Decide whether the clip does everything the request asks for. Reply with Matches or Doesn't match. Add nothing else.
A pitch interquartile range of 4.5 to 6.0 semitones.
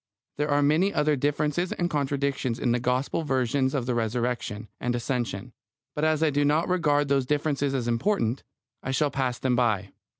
Doesn't match